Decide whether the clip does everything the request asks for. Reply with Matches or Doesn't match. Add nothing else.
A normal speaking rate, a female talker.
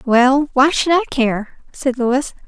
Matches